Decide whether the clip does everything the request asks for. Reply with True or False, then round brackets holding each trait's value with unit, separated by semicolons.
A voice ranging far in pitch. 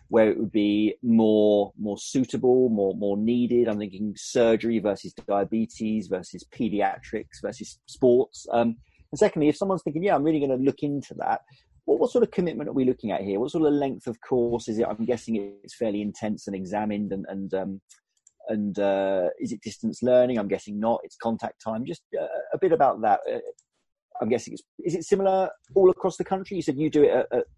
True (6.5 semitones)